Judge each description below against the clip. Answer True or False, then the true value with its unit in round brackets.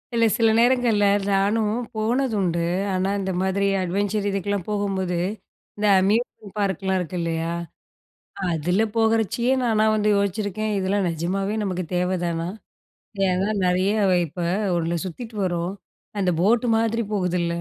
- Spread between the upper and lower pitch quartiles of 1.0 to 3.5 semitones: True (3.1 semitones)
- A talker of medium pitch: False (195 Hz)